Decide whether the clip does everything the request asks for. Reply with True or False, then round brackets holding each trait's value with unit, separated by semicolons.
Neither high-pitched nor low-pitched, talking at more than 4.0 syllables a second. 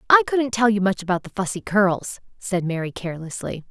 False (200 Hz; 5.5 syllables/s)